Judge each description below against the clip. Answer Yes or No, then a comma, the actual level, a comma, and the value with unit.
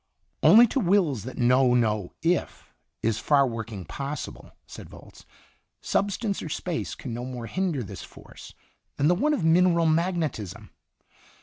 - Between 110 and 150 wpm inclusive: Yes, average, 145 wpm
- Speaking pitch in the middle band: Yes, medium, 145 Hz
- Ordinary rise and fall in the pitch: No, wide, 6.9 semitones